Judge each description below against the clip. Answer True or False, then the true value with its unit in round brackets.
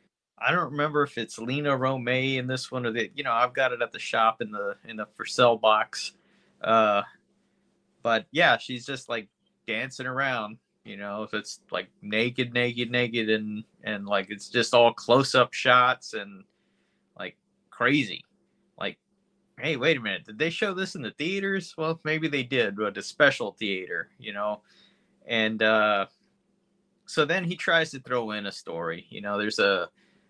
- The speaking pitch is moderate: False (125 Hz)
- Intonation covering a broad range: True (6.3 semitones)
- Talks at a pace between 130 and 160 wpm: False (180 wpm)